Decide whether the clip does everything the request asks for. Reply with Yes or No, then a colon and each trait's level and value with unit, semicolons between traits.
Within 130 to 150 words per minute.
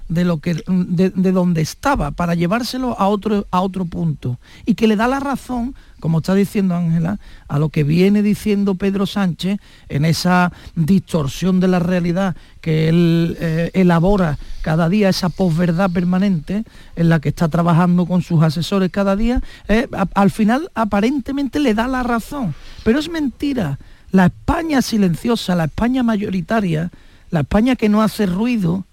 No: average, 165 wpm